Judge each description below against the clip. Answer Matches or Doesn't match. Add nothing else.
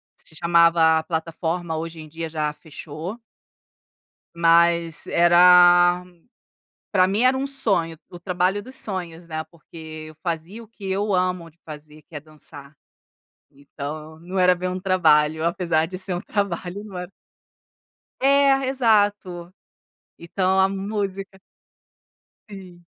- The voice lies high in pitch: Doesn't match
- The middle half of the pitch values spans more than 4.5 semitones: Doesn't match